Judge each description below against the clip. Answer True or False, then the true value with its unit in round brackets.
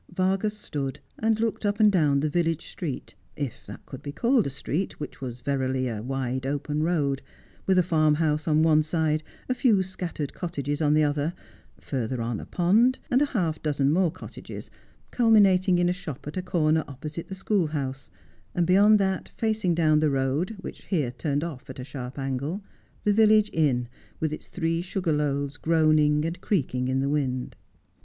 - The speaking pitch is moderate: True (155 Hz)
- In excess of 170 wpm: True (190 wpm)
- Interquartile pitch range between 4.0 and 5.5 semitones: True (4.9 semitones)